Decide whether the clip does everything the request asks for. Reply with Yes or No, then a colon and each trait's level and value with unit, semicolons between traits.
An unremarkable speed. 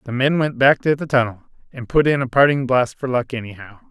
No: fast, 245 wpm